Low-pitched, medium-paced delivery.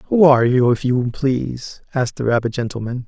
Yes: low, 125 Hz; average, 195 wpm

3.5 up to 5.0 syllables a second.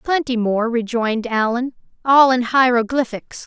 Yes: 4.6 syllables/s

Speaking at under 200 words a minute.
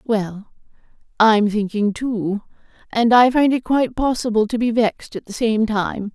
Yes: average, 165 wpm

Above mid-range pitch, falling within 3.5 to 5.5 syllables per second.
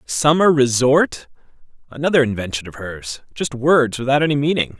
No: low, 130 Hz; 5.0 syllables/s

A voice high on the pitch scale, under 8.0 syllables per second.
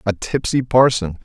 No: low, 115 Hz; 4.6 syllables/s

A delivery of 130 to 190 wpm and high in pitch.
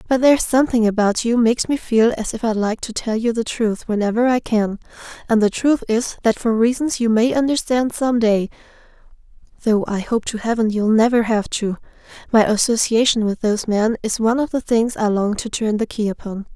No: fast, 205 wpm; high, 225 Hz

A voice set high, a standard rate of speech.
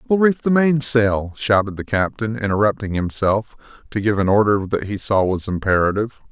No: low, 110 Hz; average, 170 wpm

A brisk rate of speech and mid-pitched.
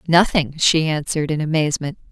No: average, 140 wpm; medium, 155 Hz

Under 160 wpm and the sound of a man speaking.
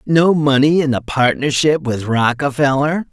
Yes: slow, 135 wpm; male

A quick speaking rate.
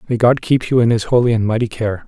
Yes: fast, 290 wpm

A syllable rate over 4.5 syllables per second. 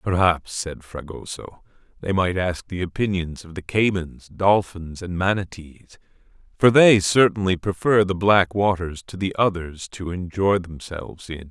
No: 4.4 syllables/s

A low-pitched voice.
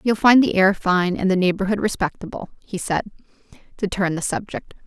No: high, 195 Hz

